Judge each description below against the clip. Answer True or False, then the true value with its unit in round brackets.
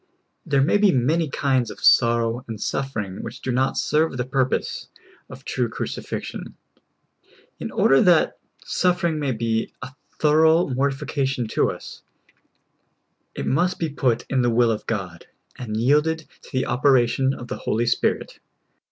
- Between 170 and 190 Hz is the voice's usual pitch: False (130 Hz)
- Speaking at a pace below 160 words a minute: True (150 wpm)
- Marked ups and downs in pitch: False (4.1 semitones)